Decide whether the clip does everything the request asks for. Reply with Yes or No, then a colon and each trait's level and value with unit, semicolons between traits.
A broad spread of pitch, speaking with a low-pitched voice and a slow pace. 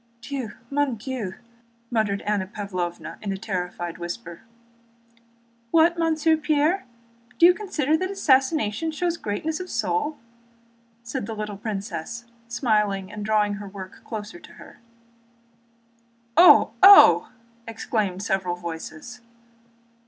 No: wide, 7.6 semitones; high, 220 Hz; slow, 115 wpm